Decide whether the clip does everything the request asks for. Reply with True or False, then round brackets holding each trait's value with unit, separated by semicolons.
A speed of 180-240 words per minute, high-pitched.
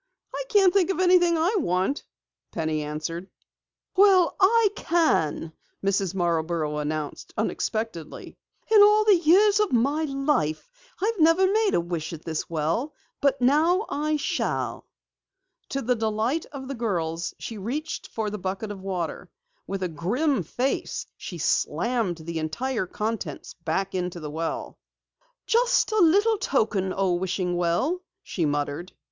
False (145 wpm; 220 Hz)